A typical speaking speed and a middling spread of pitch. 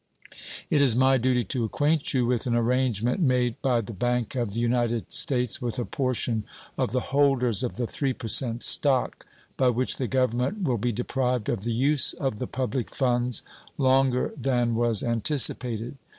No: average, 170 wpm; narrow, 1.9 semitones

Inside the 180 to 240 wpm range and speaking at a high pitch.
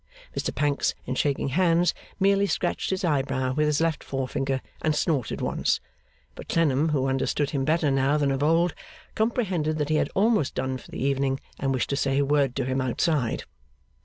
No: average, 190 wpm; medium, 145 Hz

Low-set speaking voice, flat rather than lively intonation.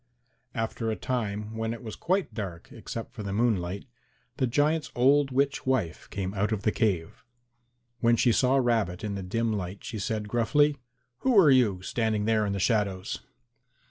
No: low, 110 Hz; average, 3.9 semitones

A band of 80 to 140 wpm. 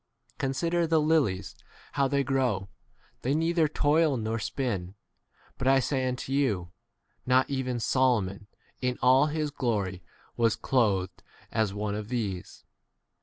Yes: slow, 135 wpm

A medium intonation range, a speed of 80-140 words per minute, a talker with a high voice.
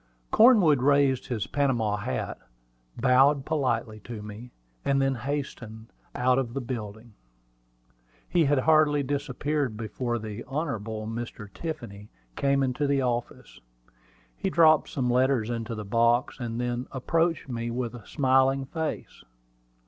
No: average, 3.4 semitones; slow, 135 wpm; low, 130 Hz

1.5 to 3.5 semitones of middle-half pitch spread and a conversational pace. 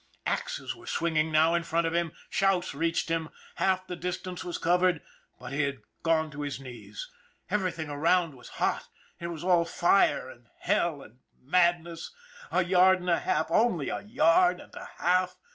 Yes: narrow, 2.4 semitones; average, 180 wpm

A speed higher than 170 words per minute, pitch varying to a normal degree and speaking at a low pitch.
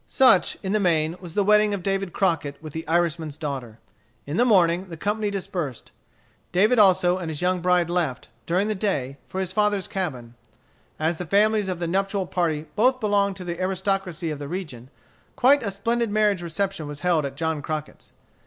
No: average, 190 wpm; average, 3.9 semitones; medium, 180 Hz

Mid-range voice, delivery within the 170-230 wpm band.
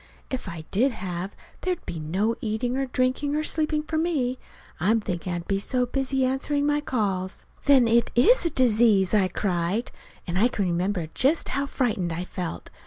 No: high, 230 Hz; average, 180 wpm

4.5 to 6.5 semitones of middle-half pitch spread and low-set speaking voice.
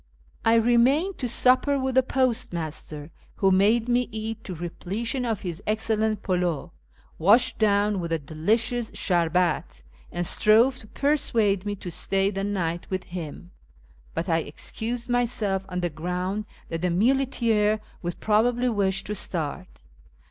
No: average, 4.9 semitones; high, 205 Hz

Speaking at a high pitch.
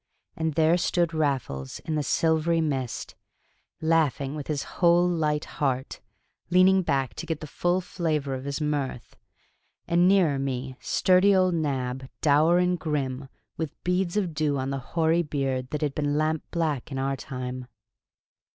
No: medium, 150 Hz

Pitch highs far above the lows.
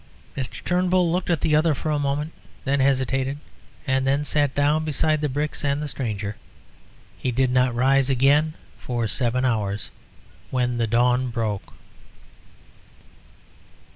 No: average, 3.1 semitones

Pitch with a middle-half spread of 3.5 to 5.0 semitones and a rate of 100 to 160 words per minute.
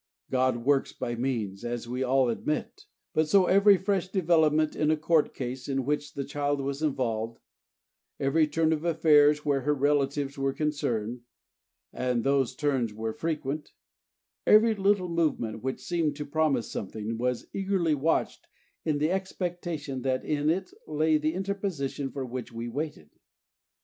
Yes: average, 3.8 semitones; average, 155 wpm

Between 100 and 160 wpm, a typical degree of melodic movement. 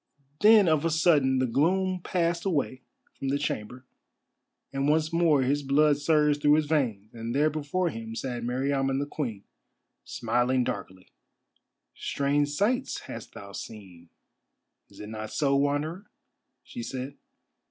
Yes: average, 140 wpm; average, 3.9 semitones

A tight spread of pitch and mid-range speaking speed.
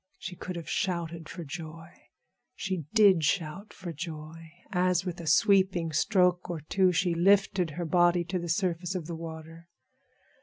Yes: narrow, 2.1 semitones; average, 160 wpm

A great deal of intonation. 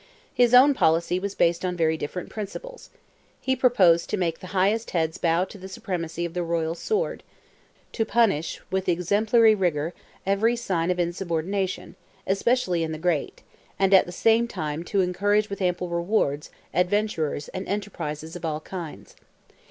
No: average, 3.6 semitones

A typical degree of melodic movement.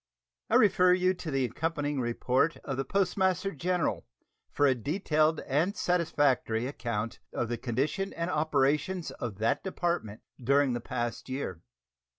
No: wide, 6.2 semitones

